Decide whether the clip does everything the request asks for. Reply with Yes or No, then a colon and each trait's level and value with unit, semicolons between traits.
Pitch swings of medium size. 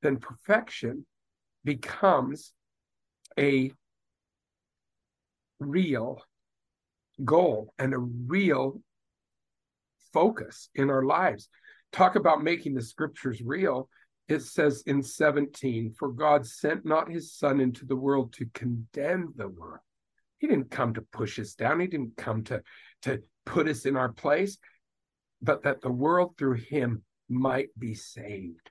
Yes: average, 4.0 semitones